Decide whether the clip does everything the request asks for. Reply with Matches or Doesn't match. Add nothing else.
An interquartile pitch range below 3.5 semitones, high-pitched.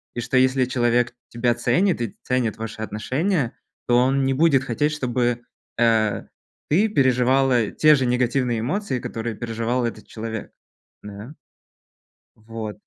Doesn't match